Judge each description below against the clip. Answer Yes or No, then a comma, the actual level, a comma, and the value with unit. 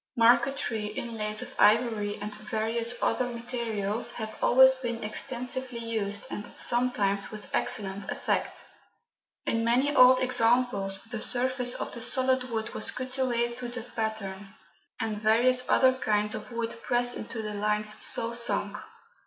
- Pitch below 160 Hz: No, high, 230 Hz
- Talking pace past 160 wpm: No, average, 145 wpm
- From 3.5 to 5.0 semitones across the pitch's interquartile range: No, average, 2.7 semitones